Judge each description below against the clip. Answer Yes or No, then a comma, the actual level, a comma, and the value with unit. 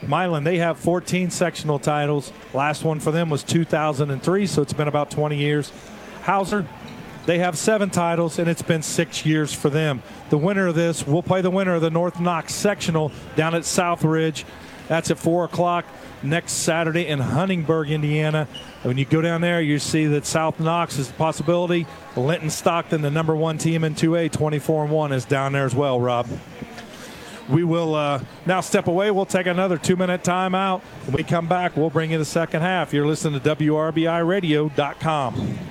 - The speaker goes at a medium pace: Yes, average, 185 wpm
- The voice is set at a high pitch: No, medium, 160 Hz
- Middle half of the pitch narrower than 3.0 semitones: Yes, narrow, 2.5 semitones